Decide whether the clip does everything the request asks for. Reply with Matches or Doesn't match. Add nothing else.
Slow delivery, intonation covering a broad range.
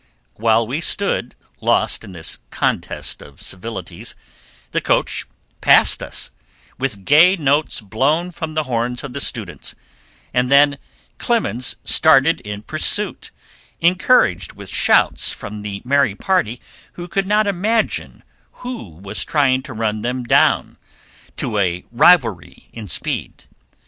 Matches